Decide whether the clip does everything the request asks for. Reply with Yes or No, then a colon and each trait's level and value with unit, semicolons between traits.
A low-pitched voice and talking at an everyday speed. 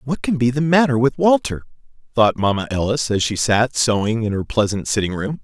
No: low, 120 Hz; fast, 210 wpm